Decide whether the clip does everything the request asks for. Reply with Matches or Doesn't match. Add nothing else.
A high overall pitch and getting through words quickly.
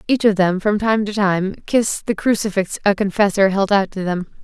Matches